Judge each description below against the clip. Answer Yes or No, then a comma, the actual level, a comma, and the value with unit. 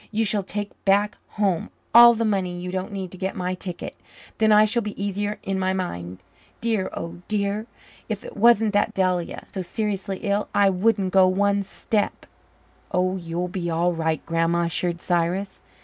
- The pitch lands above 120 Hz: Yes, high, 190 Hz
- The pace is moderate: Yes, average, 180 wpm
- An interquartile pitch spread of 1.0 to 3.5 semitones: Yes, narrow, 2.5 semitones